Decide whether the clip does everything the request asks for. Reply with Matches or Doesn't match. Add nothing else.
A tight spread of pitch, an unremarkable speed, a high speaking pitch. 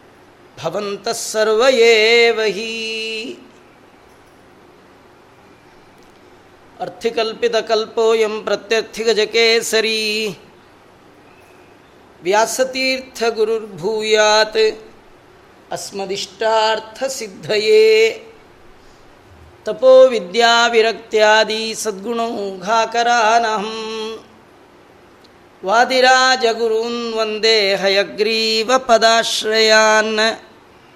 Doesn't match